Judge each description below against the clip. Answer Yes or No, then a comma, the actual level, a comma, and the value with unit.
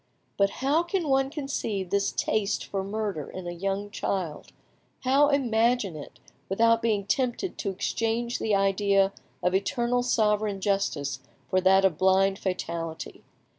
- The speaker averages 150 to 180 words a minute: No, average, 140 wpm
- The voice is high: Yes, high, 200 Hz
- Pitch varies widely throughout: No, average, 3.7 semitones